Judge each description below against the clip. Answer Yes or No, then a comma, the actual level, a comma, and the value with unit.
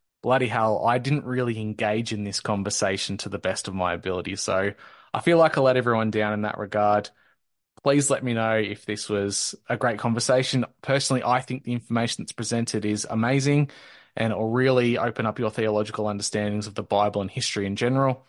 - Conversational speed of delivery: Yes, average, 195 wpm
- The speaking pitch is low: Yes, low, 110 Hz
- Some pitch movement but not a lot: Yes, average, 3.4 semitones